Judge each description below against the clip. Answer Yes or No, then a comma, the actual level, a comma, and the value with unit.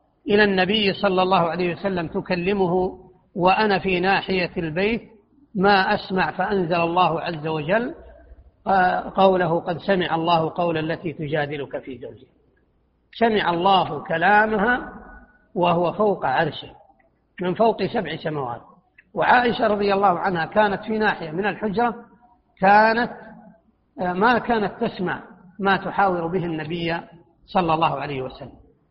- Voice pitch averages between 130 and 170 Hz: No, high, 190 Hz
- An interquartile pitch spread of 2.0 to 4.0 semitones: Yes, average, 3.7 semitones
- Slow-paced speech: No, average, 120 wpm